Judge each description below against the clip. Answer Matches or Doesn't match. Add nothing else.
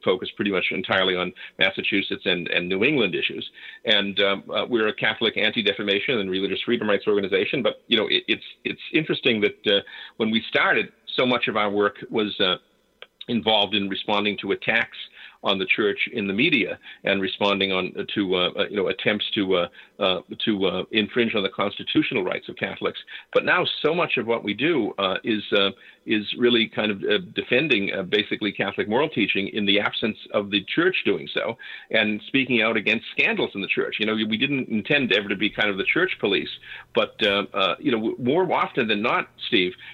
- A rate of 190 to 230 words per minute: Matches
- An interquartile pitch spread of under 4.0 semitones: Matches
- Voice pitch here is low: Matches